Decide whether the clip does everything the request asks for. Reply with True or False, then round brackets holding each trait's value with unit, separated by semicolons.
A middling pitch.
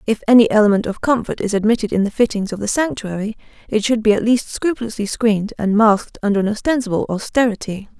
False (215 Hz)